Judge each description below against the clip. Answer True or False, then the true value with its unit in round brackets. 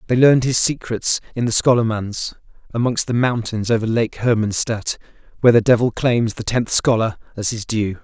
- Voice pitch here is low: True (115 Hz)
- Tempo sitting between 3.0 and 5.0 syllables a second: False (5.4 syllables/s)